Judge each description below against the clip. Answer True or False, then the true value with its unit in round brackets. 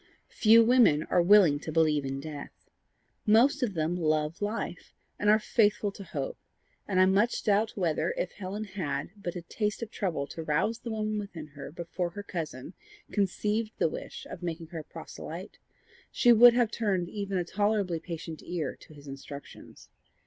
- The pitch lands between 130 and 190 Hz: True (185 Hz)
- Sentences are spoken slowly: False (180 wpm)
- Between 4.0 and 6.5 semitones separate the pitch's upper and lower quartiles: True (5.0 semitones)